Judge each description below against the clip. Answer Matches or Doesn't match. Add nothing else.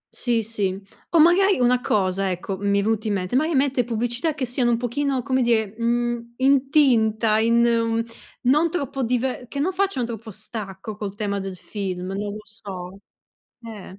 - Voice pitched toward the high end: Matches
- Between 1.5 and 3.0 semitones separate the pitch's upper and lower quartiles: Doesn't match